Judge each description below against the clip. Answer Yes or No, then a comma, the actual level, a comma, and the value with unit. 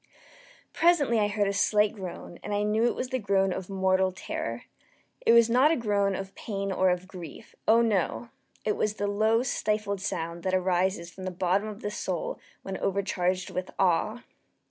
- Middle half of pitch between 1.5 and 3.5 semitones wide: Yes, narrow, 2.6 semitones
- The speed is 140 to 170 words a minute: No, average, 190 wpm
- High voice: Yes, high, 200 Hz